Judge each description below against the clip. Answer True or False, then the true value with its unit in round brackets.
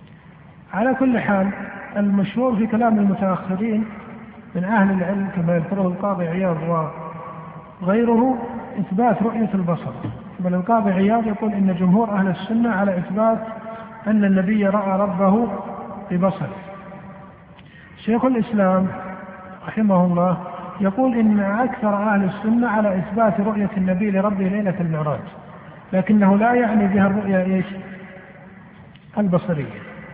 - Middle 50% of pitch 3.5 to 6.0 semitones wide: False (2.8 semitones)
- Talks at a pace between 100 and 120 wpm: True (110 wpm)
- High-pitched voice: True (195 Hz)